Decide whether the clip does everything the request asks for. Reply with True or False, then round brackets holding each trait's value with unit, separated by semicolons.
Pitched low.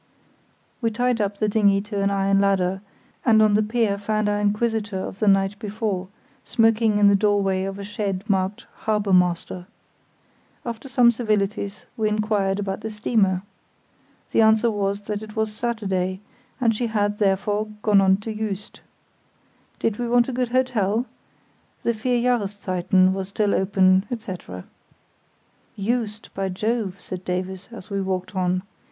False (205 Hz)